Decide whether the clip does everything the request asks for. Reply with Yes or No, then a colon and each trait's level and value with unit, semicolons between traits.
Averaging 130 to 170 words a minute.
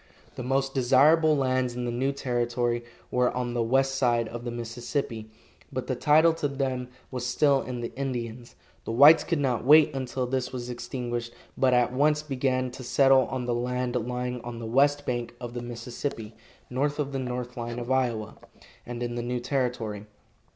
No: average, 185 wpm